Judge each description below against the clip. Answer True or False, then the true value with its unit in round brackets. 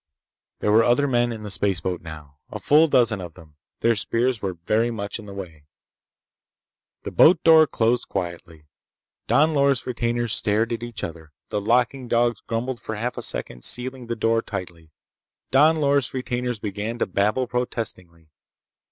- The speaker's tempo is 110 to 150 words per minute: False (165 wpm)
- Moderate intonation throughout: True (4.1 semitones)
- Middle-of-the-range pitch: False (115 Hz)